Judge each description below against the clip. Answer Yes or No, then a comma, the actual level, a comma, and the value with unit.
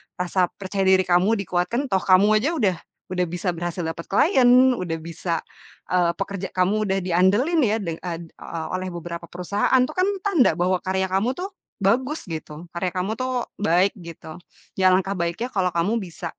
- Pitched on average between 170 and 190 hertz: Yes, medium, 185 Hz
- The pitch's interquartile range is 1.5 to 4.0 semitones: Yes, average, 3.6 semitones